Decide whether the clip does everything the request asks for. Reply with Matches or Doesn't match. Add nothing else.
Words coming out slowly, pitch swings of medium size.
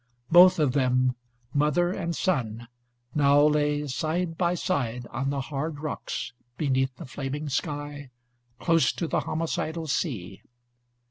Matches